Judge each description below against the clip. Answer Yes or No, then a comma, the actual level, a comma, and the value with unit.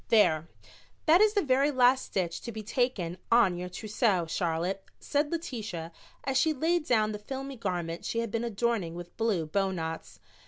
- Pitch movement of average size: No, wide, 6.6 semitones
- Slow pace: No, average, 170 wpm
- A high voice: Yes, high, 215 Hz